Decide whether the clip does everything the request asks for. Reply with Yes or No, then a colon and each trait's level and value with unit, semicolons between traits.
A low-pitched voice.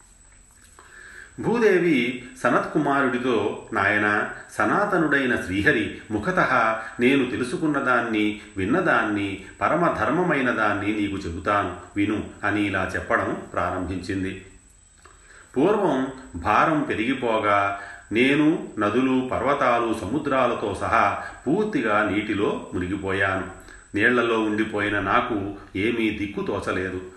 Yes: low, 105 Hz